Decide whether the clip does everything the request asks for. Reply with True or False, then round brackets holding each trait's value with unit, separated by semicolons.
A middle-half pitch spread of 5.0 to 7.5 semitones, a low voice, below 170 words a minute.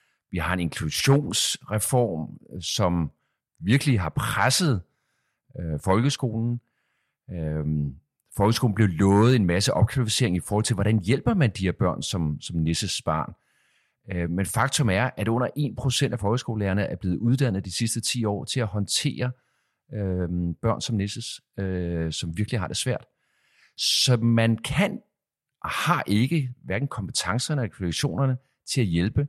True (5.6 semitones; 110 Hz; 150 wpm)